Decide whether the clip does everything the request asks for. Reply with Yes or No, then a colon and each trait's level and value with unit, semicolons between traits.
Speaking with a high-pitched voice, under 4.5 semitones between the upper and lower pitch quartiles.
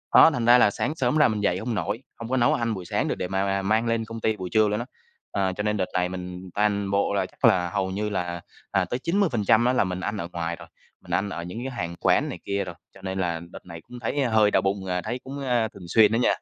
No: low, 100 Hz; average, 3.9 semitones